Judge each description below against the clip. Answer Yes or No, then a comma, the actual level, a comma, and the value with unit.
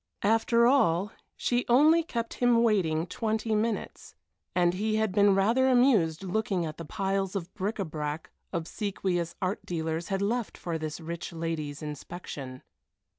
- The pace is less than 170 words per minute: Yes, average, 150 wpm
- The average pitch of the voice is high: Yes, high, 195 Hz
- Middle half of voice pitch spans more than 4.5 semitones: Yes, average, 5.1 semitones